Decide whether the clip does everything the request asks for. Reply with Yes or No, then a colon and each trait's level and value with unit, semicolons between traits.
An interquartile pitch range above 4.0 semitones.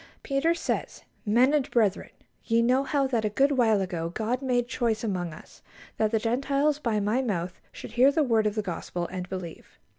Yes: average, 4.5 semitones